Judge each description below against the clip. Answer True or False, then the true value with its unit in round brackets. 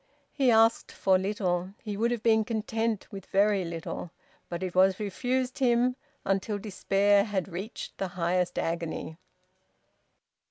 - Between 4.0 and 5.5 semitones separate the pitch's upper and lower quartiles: False (3.4 semitones)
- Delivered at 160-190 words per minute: False (135 wpm)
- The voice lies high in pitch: True (200 Hz)